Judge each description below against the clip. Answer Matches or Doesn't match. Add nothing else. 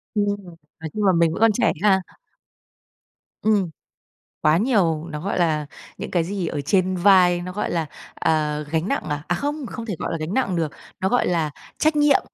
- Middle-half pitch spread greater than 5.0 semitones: Doesn't match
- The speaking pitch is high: Doesn't match